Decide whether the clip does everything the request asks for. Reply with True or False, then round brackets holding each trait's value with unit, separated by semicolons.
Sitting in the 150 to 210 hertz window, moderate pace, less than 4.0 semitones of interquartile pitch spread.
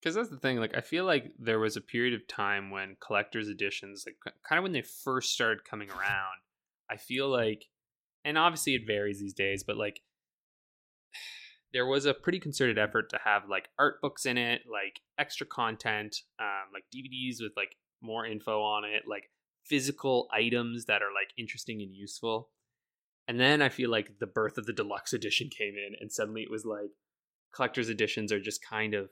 False (110 Hz; 195 wpm; 3.2 semitones)